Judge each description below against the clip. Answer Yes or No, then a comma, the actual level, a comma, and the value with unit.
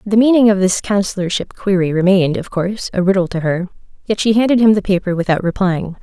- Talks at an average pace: No, fast, 210 wpm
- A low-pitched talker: No, high, 190 Hz